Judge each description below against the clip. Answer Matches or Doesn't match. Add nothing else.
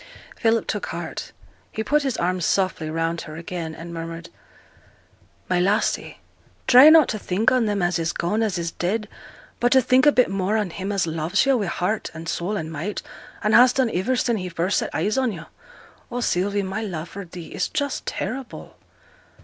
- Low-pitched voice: Doesn't match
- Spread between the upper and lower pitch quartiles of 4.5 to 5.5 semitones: Matches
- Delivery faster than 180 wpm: Matches